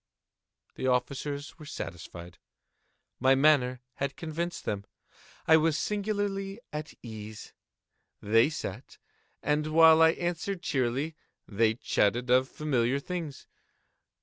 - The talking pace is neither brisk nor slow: No, slow, 110 wpm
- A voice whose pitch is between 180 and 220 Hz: No, medium, 140 Hz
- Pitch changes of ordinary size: Yes, average, 5.0 semitones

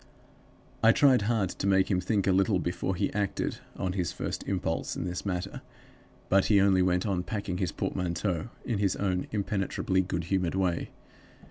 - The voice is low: Yes, very low, 95 Hz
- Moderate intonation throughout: No, narrow, 1.9 semitones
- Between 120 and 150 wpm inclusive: No, average, 175 wpm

